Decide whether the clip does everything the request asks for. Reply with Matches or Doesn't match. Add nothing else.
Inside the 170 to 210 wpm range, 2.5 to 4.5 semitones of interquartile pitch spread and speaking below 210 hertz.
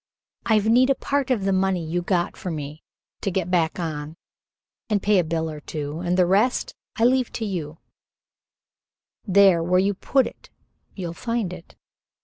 Matches